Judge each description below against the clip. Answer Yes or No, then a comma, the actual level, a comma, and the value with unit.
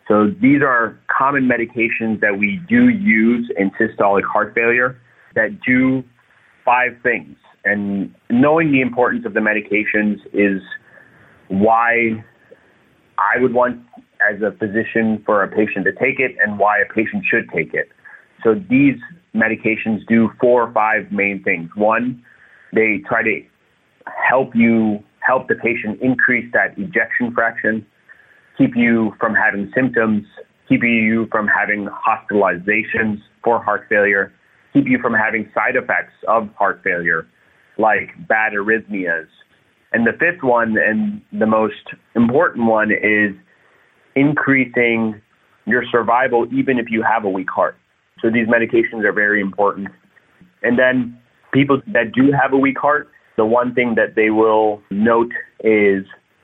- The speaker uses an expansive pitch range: No, average, 3.0 semitones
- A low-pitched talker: Yes, low, 115 Hz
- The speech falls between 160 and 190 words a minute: No, average, 145 wpm